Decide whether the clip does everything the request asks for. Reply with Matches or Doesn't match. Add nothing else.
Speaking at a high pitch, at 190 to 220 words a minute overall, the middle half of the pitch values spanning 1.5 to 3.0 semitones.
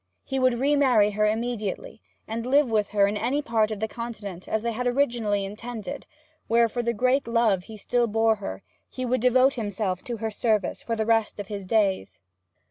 Matches